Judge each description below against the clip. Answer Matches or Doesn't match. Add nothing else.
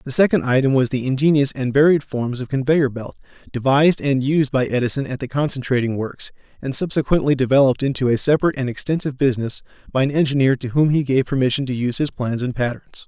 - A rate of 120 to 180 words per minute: Doesn't match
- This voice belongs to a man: Matches